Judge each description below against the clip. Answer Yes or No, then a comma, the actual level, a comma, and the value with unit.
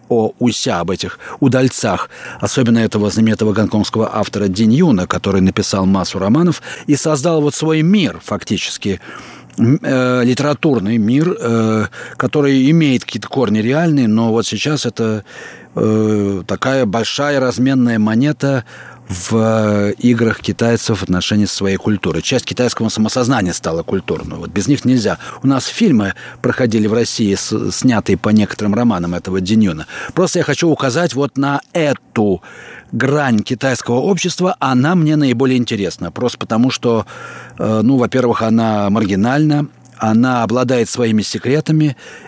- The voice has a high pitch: No, low, 115 Hz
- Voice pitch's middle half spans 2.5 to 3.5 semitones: No, average, 4.1 semitones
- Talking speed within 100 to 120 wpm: No, average, 130 wpm